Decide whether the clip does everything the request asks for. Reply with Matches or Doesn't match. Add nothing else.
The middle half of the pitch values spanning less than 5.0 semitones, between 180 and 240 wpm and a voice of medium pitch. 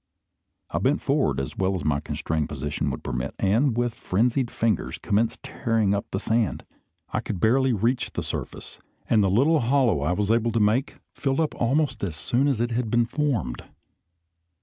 Doesn't match